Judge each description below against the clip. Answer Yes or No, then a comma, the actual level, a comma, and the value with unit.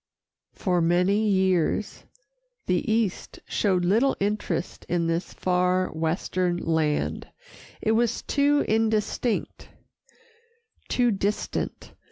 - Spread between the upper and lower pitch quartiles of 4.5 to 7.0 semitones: No, average, 3.7 semitones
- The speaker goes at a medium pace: No, slow, 95 wpm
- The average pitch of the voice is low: No, high, 190 Hz